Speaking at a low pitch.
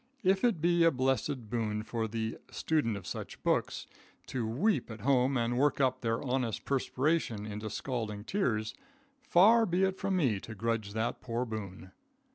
Yes: low, 120 Hz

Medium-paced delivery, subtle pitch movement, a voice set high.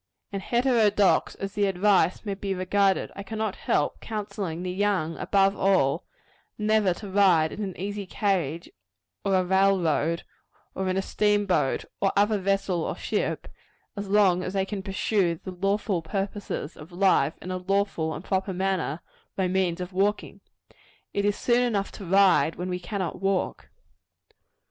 Yes: average, 160 wpm; narrow, 2.0 semitones; high, 195 Hz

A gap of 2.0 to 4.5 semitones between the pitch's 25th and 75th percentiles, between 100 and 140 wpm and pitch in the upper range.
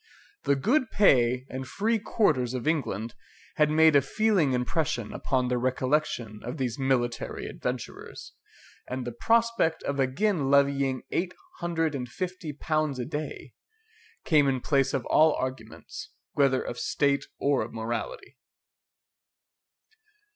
No: average, 4.1 semitones; slow, 135 wpm; medium, 140 Hz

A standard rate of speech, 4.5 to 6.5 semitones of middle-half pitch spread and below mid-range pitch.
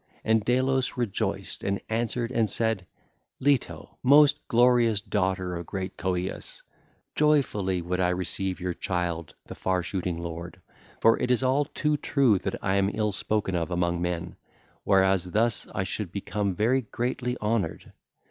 Yes: average, 150 wpm; average, 4.9 semitones; low, 100 Hz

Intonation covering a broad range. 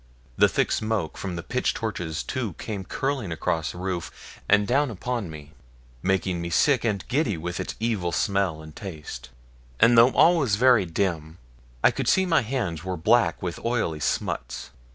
Yes: wide, 5.8 semitones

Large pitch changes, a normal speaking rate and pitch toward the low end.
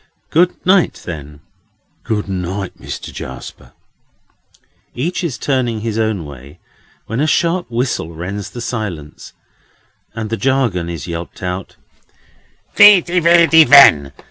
No: wide, 8.7 semitones; slow, 120 wpm; low, 110 Hz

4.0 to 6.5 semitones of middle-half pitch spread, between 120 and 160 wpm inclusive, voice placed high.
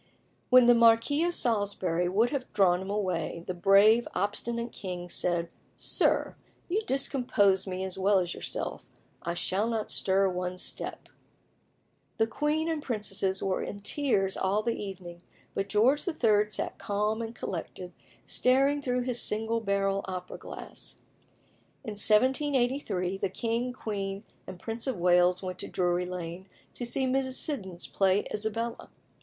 Yes: average, 4.4 semitones; average, 150 wpm; high, 205 Hz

